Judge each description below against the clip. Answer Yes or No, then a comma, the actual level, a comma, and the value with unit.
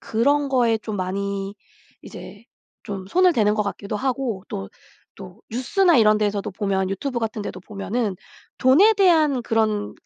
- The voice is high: Yes, high, 215 Hz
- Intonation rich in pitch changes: No, average, 4.6 semitones